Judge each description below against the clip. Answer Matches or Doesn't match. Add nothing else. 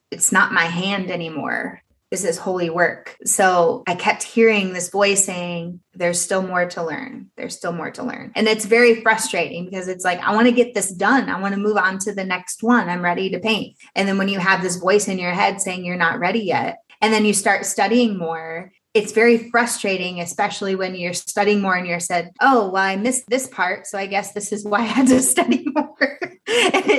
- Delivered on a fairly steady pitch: Doesn't match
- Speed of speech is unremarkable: Doesn't match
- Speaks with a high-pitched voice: Matches